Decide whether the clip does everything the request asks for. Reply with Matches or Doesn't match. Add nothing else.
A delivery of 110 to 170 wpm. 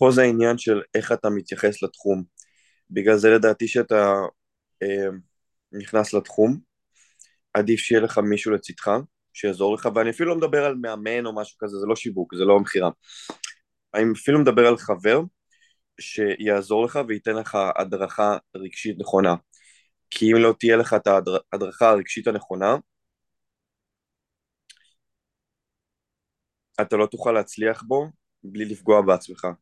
Matches